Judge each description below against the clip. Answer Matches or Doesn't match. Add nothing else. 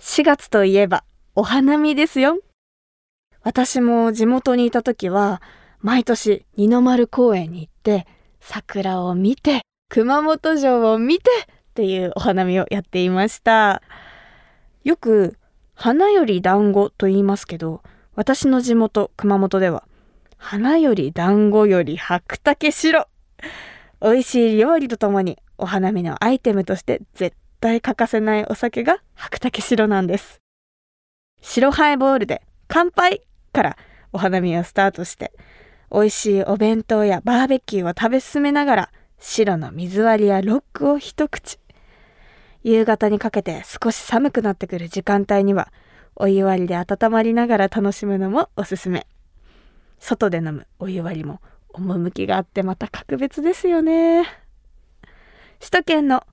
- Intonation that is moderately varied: Matches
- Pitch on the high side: Matches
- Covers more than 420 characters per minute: Doesn't match